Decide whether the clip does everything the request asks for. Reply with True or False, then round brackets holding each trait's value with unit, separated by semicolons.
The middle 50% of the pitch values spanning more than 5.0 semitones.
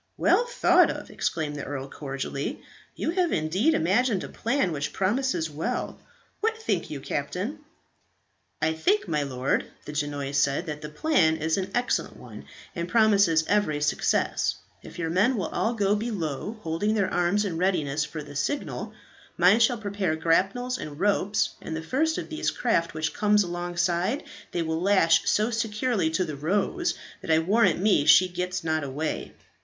True (5.5 semitones)